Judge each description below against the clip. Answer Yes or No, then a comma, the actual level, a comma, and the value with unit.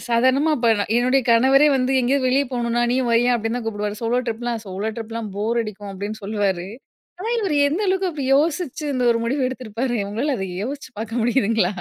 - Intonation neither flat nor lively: Yes, average, 3.4 semitones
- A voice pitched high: Yes, high, 240 Hz